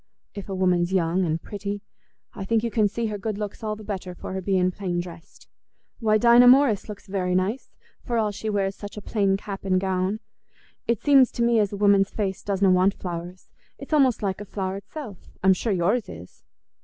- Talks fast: Yes, fast, 210 wpm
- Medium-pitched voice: No, high, 200 Hz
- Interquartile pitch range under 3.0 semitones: Yes, narrow, 2.6 semitones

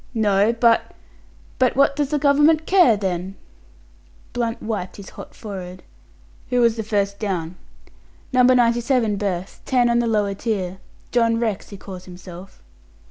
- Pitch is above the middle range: Yes, high, 220 Hz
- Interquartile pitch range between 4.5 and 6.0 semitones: No, average, 3.9 semitones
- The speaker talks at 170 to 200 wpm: No, average, 150 wpm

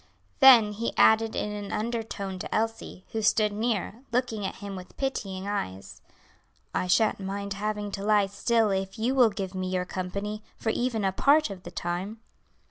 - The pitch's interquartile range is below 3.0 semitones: Yes, narrow, 2.6 semitones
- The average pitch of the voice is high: Yes, high, 205 Hz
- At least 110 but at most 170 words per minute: No, average, 180 wpm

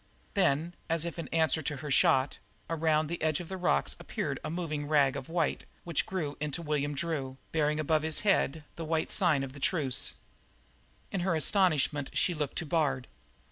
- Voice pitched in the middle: Yes, medium, 155 Hz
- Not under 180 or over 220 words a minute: Yes, average, 185 wpm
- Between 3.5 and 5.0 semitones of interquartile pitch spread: No, narrow, 2.6 semitones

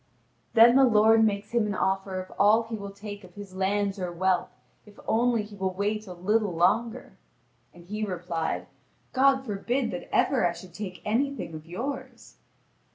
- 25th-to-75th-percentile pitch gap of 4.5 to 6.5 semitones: No, average, 3.3 semitones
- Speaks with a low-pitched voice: No, high, 205 Hz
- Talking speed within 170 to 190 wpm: Yes, average, 175 wpm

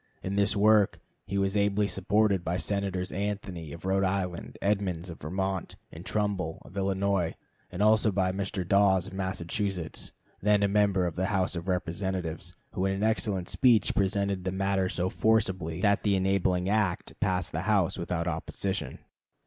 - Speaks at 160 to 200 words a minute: Yes, average, 165 wpm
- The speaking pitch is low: Yes, very low, 95 Hz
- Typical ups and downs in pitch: No, narrow, 1.9 semitones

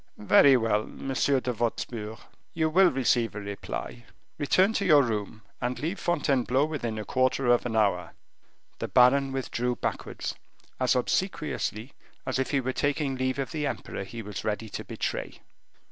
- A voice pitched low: Yes, low, 125 Hz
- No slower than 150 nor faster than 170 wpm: Yes, average, 160 wpm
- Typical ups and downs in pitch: Yes, average, 4.0 semitones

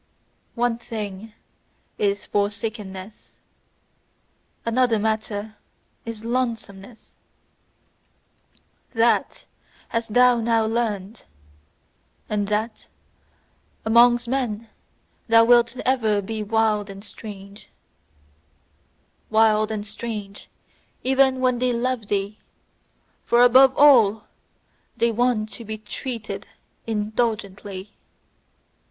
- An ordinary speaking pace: No, slow, 85 wpm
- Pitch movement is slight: Yes, narrow, 2.3 semitones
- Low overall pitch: No, high, 220 Hz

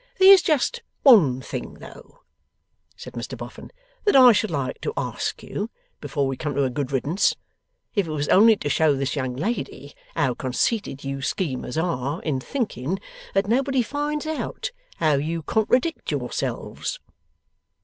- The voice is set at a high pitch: No, medium, 160 Hz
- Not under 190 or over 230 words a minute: No, average, 155 wpm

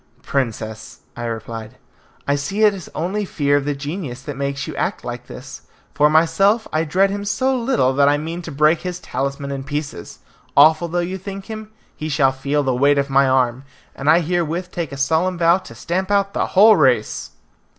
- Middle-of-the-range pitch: Yes, medium, 155 Hz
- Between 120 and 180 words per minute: No, average, 200 wpm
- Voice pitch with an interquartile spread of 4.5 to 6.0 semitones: Yes, average, 4.9 semitones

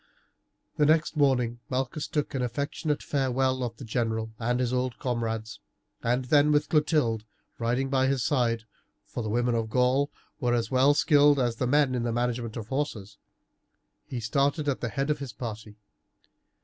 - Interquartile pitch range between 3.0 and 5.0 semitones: Yes, average, 3.3 semitones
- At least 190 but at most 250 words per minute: No, average, 175 wpm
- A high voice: No, low, 125 Hz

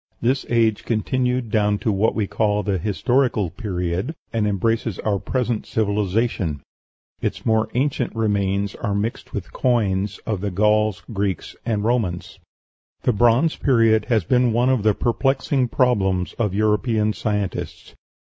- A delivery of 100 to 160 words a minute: Yes, average, 140 wpm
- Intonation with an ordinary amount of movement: Yes, average, 3.0 semitones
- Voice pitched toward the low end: Yes, low, 110 Hz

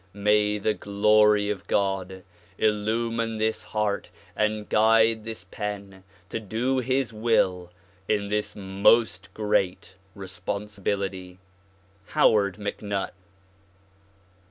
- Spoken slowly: Yes, slow, 100 wpm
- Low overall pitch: Yes, low, 105 Hz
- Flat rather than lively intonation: Yes, narrow, 2.0 semitones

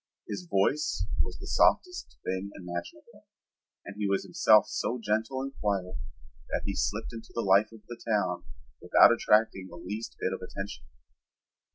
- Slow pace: No, average, 160 wpm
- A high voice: No, low, 105 Hz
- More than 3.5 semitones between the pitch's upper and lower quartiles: No, average, 3.2 semitones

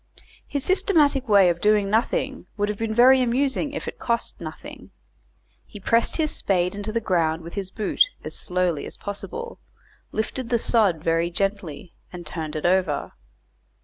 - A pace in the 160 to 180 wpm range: Yes, average, 165 wpm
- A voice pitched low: No, high, 205 Hz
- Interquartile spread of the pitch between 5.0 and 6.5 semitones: Yes, wide, 5.5 semitones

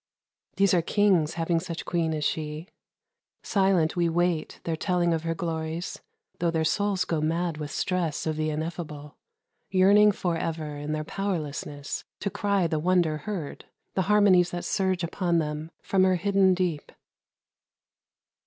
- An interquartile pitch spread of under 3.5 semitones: Yes, average, 3.0 semitones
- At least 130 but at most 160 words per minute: Yes, average, 155 wpm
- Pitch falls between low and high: Yes, medium, 170 Hz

